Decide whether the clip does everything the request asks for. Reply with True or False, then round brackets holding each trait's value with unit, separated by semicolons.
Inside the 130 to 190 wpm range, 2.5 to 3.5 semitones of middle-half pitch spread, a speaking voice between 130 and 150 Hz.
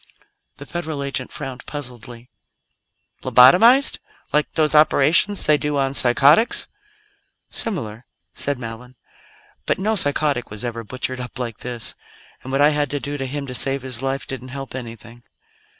True (150 wpm; 3.0 semitones; 135 Hz)